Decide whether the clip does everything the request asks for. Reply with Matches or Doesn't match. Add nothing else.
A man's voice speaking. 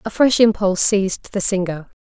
Doesn't match